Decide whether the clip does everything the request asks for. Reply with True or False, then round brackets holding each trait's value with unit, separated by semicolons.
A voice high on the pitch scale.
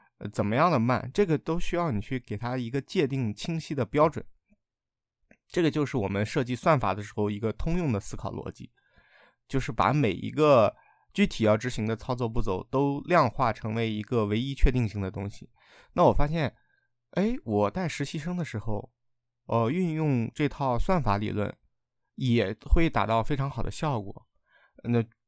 False (125 Hz)